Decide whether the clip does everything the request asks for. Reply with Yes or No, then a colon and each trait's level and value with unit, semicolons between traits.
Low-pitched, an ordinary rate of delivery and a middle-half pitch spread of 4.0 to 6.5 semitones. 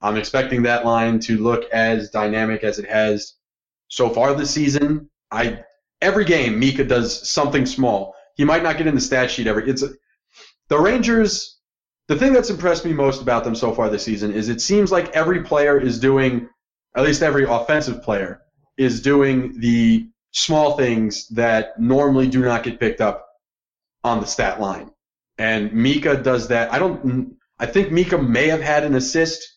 Yes: low, 130 Hz; average, 185 wpm; average, 4.8 semitones